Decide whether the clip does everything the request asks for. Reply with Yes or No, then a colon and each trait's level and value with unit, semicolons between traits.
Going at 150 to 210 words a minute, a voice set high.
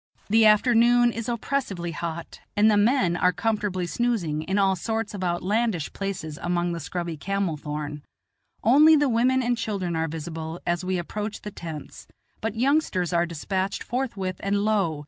Yes: average, 165 wpm; high, 195 Hz